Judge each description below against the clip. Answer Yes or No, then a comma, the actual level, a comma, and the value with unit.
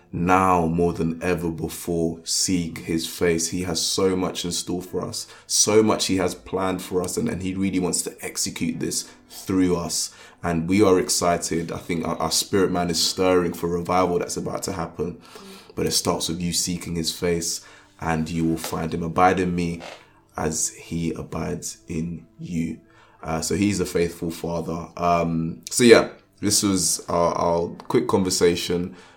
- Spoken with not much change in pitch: Yes, narrow, 1.8 semitones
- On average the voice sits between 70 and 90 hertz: Yes, very low, 85 Hz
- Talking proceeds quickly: No, average, 180 wpm